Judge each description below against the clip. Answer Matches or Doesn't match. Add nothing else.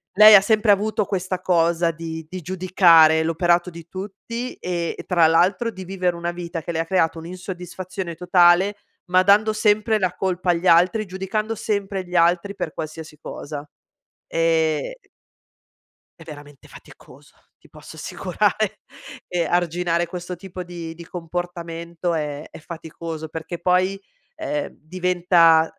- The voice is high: Doesn't match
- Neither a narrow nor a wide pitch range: Doesn't match